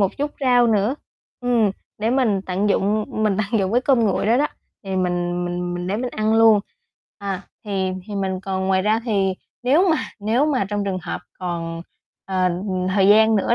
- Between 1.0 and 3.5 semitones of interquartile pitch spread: Yes, average, 3.2 semitones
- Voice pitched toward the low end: No, high, 205 Hz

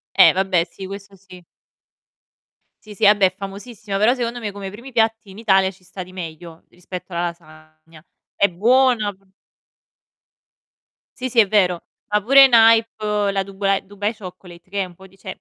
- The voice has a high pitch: Yes, high, 195 Hz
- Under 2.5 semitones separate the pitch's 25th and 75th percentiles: No, average, 2.8 semitones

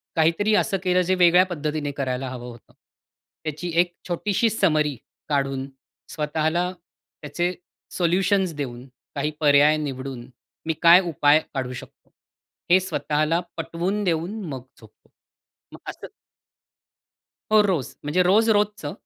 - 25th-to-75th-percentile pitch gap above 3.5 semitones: Yes, average, 4.2 semitones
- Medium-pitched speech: Yes, medium, 160 Hz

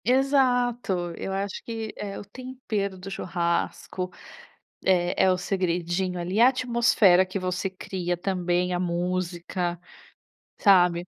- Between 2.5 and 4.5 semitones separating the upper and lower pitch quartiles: Yes, average, 2.8 semitones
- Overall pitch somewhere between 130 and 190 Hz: Yes, medium, 185 Hz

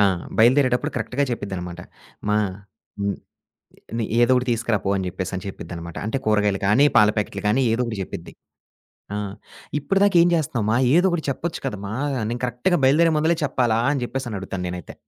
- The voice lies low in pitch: Yes, low, 115 Hz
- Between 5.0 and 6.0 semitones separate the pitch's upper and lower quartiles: Yes, wide, 5.5 semitones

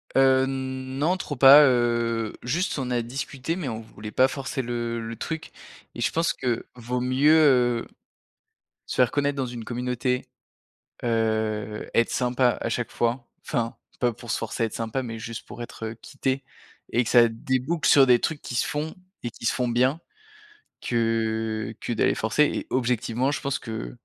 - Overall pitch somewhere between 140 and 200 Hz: No, low, 125 Hz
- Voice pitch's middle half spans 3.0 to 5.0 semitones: No, narrow, 2.5 semitones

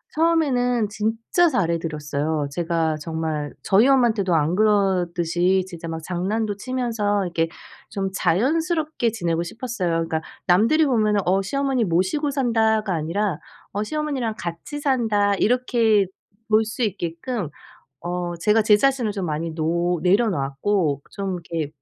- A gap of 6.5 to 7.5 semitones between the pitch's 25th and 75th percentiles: No, wide, 5.6 semitones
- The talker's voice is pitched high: Yes, high, 200 Hz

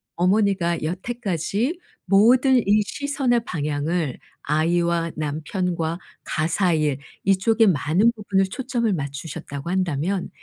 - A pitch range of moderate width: Yes, average, 5.0 semitones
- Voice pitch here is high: No, medium, 180 Hz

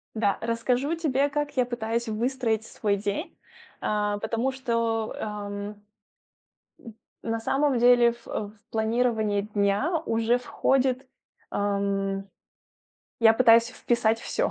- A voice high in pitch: Yes, high, 230 Hz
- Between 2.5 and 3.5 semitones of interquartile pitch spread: Yes, average, 3.0 semitones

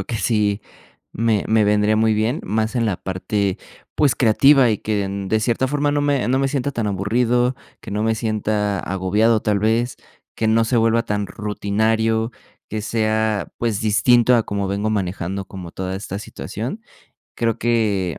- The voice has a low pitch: Yes, low, 110 Hz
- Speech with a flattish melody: Yes, narrow, 2.3 semitones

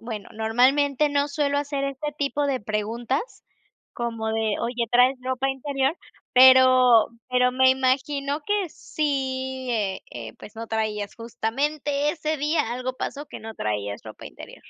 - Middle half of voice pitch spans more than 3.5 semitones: Yes, average, 3.9 semitones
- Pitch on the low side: No, very high, 260 Hz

